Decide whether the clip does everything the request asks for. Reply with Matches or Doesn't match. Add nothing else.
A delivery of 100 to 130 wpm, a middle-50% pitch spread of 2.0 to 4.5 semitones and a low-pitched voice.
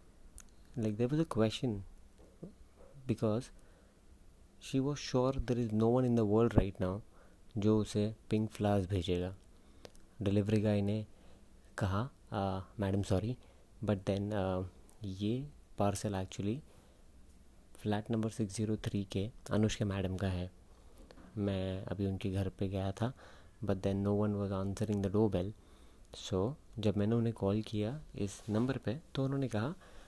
Doesn't match